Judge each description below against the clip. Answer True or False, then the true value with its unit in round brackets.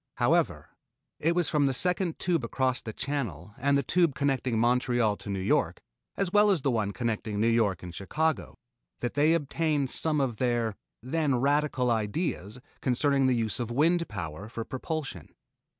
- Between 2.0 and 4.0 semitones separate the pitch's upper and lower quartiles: False (5.1 semitones)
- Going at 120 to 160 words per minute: False (170 wpm)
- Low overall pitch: True (130 Hz)